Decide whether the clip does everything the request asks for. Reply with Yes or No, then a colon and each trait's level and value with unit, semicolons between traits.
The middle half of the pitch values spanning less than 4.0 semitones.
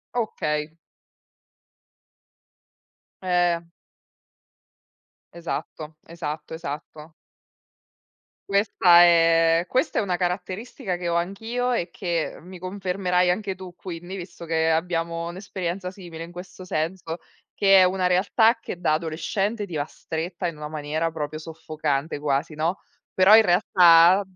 Yes: narrow, 2.5 semitones